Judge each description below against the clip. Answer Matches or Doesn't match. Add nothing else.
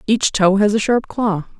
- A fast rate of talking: Matches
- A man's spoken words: Doesn't match